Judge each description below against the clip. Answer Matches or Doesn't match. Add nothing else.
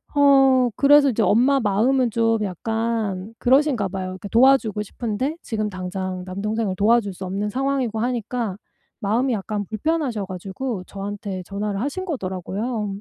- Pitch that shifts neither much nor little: Matches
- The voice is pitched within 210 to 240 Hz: Matches